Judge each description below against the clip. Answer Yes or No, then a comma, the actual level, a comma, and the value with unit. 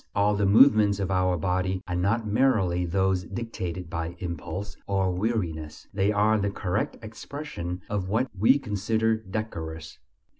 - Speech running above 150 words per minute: No, average, 145 wpm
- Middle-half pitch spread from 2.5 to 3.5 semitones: Yes, average, 3.2 semitones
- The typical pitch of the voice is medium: No, low, 100 Hz